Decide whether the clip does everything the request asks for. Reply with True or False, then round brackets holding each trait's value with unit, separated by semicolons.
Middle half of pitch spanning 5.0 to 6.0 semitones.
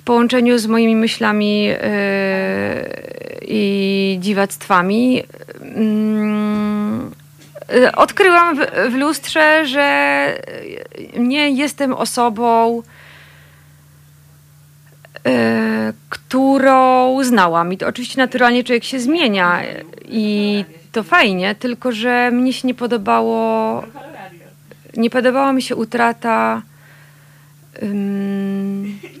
True (5.3 semitones)